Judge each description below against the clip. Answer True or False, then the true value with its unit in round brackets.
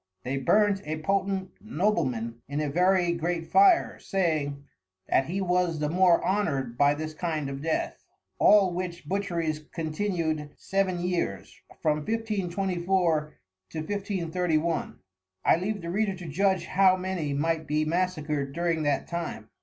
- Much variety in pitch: False (3.7 semitones)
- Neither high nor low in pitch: True (170 Hz)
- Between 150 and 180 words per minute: False (140 wpm)